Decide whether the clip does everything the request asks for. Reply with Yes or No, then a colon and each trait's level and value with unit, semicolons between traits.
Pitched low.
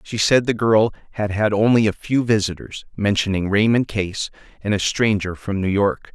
Yes: low, 105 Hz